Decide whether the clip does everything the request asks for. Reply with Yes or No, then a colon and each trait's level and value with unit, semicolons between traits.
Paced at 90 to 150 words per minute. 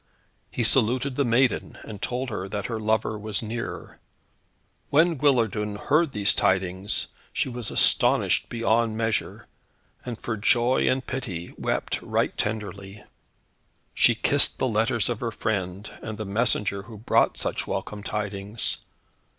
Yes: average, 140 wpm